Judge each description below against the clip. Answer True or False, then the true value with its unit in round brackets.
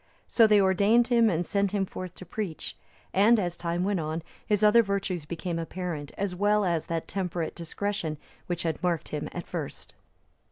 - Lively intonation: False (3.4 semitones)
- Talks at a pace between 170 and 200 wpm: True (185 wpm)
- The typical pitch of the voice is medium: True (180 Hz)